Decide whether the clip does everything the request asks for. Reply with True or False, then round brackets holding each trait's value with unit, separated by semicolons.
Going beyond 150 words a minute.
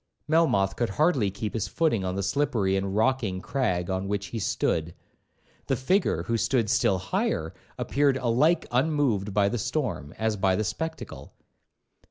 True (160 wpm)